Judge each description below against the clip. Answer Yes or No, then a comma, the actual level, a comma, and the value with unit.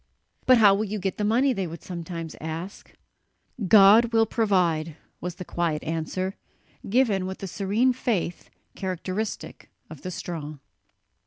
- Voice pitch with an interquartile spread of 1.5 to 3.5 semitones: No, average, 4.3 semitones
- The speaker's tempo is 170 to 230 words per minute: No, average, 145 wpm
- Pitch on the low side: No, high, 190 Hz